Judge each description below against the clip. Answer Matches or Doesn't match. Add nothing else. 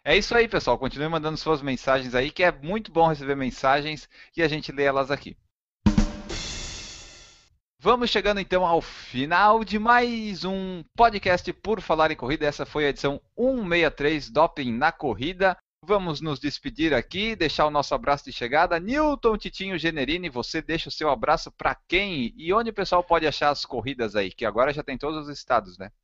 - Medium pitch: Matches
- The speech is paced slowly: Doesn't match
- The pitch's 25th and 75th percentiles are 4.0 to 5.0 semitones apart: Doesn't match